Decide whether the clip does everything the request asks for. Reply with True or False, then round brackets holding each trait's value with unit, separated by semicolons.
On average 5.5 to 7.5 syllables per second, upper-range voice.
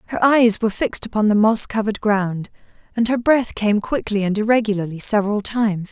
True (6.0 syllables/s; 215 Hz)